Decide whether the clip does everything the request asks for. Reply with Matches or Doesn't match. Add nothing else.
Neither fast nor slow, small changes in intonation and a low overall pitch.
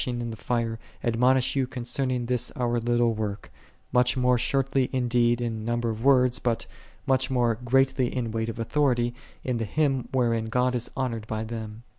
Matches